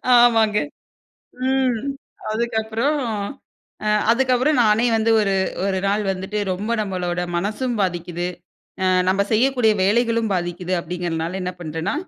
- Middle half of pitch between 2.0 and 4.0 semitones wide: No, average, 4.4 semitones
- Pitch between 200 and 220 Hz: Yes, high, 210 Hz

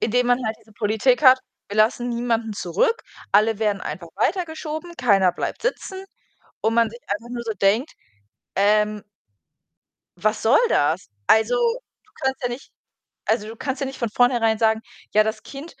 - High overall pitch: Yes, high, 230 Hz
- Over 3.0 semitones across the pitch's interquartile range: Yes, average, 3.7 semitones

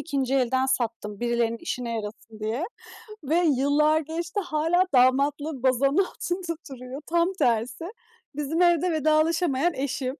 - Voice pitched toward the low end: No, very high, 280 Hz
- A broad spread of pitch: No, average, 4.6 semitones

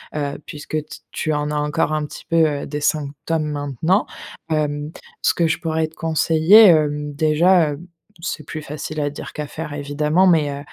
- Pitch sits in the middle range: Yes, medium, 150 Hz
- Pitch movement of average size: No, narrow, 1.6 semitones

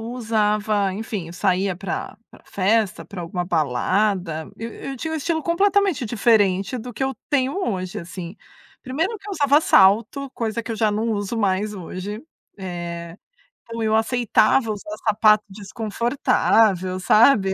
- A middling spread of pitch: Yes, average, 3.9 semitones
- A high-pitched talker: Yes, high, 215 Hz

